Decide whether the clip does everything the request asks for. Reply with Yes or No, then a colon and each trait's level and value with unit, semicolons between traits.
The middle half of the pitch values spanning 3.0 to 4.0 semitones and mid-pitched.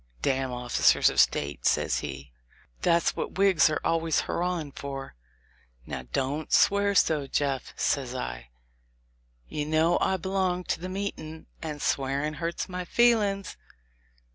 No: average, 5.0 semitones; medium, 155 Hz